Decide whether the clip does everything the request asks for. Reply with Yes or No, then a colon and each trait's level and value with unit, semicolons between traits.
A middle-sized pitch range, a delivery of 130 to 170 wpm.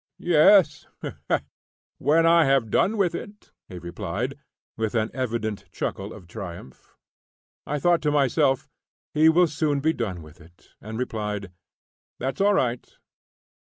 No: wide, 7.2 semitones; slow, 135 wpm